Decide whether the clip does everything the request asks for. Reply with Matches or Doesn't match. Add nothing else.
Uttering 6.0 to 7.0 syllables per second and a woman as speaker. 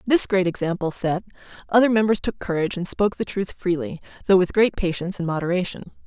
Matches